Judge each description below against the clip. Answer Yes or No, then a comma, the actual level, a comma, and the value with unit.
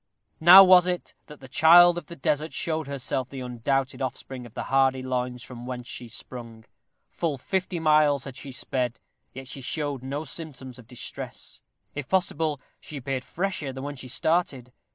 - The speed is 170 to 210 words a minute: Yes, average, 175 wpm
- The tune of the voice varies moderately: Yes, average, 3.7 semitones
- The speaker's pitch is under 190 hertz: Yes, low, 135 Hz